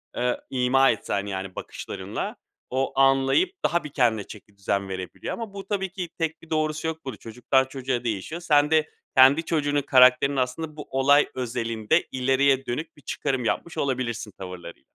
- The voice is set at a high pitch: No, low, 135 Hz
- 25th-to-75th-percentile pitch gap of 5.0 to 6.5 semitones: No, average, 4.3 semitones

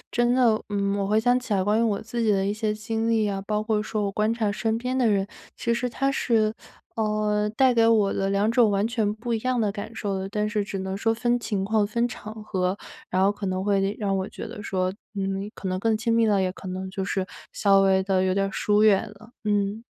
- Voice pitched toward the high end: Yes, high, 210 Hz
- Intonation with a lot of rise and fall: No, narrow, 2.4 semitones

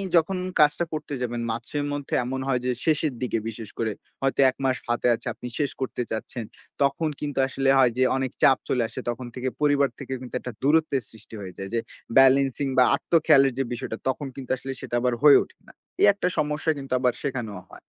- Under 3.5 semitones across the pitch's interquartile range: Yes, average, 2.8 semitones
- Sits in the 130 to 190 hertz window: Yes, low, 135 Hz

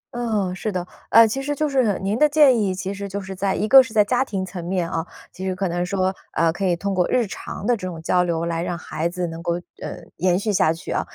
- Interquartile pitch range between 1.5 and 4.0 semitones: Yes, average, 3.7 semitones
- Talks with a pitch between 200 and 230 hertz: No, high, 190 Hz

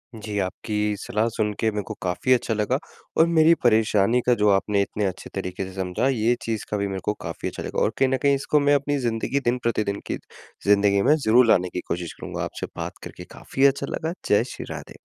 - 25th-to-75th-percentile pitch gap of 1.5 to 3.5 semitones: No, average, 4.3 semitones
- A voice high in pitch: No, low, 110 Hz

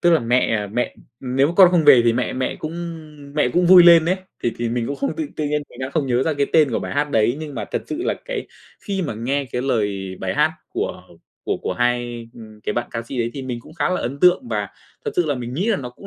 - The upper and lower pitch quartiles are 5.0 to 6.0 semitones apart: Yes, wide, 5.5 semitones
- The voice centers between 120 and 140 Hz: Yes, low, 135 Hz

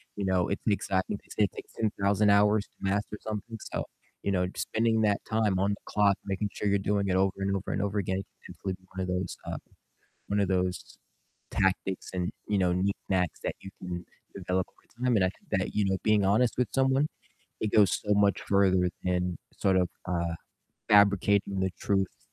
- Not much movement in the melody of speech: Yes, narrow, 1.8 semitones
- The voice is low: Yes, low, 100 Hz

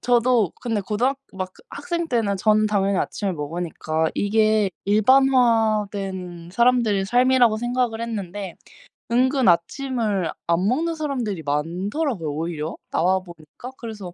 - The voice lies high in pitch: Yes, high, 210 Hz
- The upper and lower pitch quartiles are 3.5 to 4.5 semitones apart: No, average, 5.1 semitones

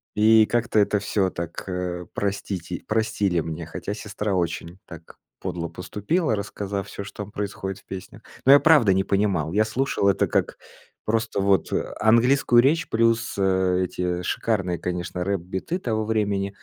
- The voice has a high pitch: No, low, 100 Hz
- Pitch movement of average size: Yes, average, 3.3 semitones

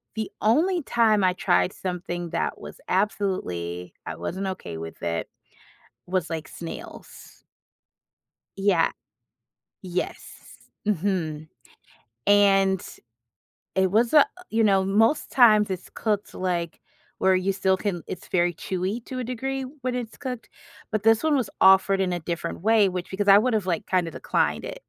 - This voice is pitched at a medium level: No, high, 195 Hz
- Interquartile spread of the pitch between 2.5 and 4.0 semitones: Yes, average, 3.6 semitones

